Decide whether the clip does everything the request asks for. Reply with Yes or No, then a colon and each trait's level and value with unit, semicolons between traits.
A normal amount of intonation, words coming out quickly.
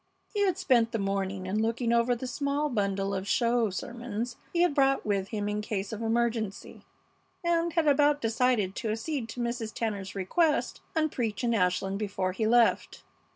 No: average, 4.2 semitones; average, 180 wpm